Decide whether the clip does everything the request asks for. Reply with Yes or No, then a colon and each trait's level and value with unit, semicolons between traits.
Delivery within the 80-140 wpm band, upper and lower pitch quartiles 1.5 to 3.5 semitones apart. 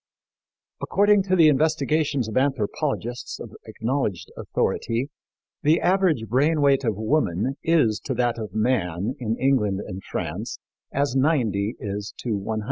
No: slow, 135 wpm; wide, 5.5 semitones